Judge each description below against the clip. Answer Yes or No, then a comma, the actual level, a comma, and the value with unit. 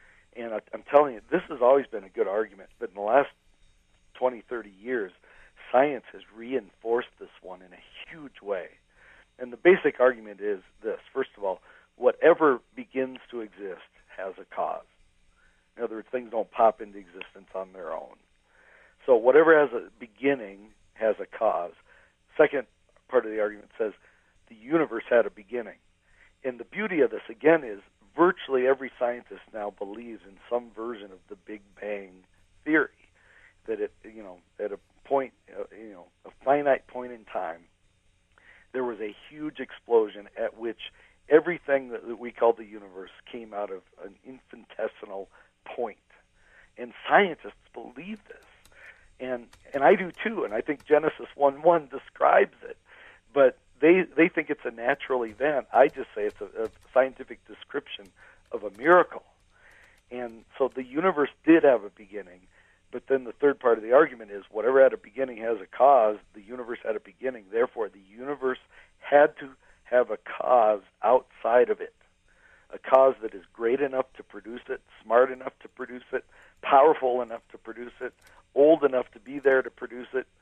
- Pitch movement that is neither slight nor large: No, wide, 5.9 semitones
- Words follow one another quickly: No, average, 170 wpm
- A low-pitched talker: Yes, low, 125 Hz